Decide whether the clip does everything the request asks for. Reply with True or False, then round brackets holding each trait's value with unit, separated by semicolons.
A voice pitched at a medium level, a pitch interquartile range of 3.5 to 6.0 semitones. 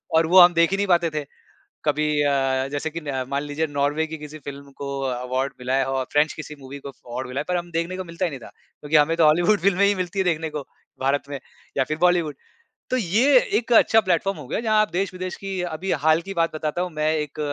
True (160 Hz; 4.1 semitones)